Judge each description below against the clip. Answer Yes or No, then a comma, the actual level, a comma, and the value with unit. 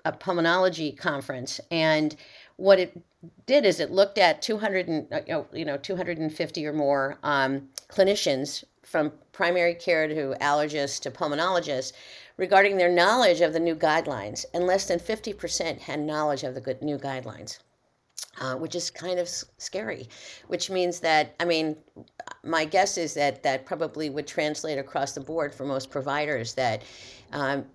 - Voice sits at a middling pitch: Yes, medium, 160 Hz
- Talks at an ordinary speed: Yes, average, 160 wpm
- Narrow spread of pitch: No, average, 3.6 semitones